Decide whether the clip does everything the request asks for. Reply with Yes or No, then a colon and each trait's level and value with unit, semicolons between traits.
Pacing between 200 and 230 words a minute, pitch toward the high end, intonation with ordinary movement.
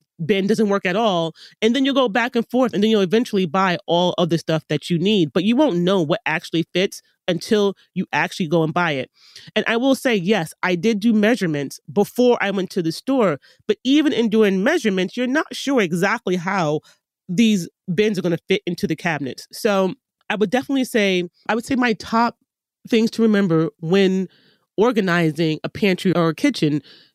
Yes: fast, 205 wpm; high, 195 Hz; average, 4.5 semitones